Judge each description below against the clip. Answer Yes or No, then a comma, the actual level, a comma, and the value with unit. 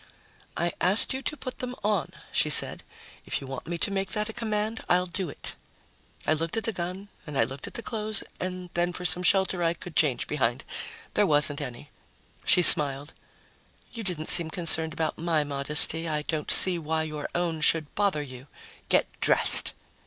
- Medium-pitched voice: Yes, medium, 170 Hz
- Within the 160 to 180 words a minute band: No, average, 190 wpm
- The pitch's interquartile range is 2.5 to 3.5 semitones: No, average, 4.2 semitones